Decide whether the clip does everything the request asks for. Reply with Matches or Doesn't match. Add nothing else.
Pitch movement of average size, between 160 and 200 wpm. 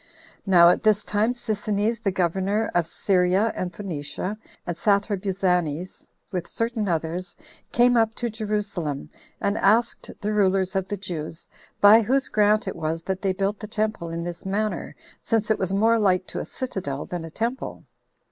Matches